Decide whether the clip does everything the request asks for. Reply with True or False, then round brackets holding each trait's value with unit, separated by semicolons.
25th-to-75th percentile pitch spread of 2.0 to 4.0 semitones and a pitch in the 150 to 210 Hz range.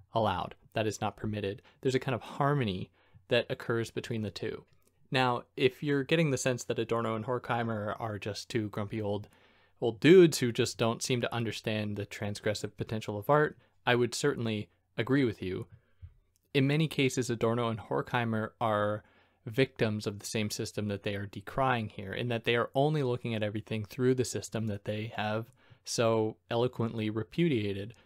False (3.0 semitones; 115 Hz)